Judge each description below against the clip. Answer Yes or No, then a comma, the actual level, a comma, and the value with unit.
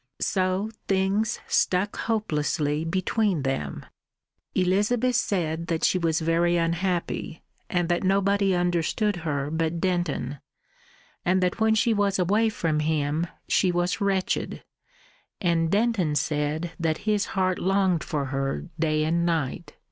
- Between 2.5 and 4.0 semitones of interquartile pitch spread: Yes, average, 3.5 semitones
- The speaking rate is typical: No, slow, 130 wpm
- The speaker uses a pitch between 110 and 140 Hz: No, medium, 175 Hz